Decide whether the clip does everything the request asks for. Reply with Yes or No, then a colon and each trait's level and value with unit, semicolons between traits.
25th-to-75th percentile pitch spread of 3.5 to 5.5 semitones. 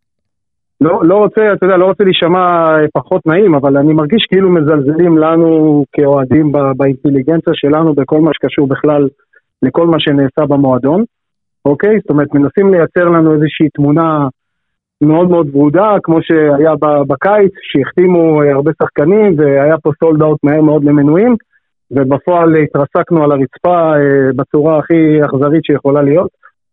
No: average, 2.8 semitones